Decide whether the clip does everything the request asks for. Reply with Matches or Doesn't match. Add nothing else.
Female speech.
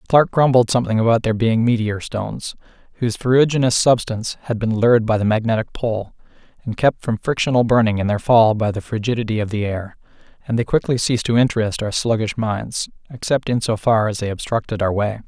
Doesn't match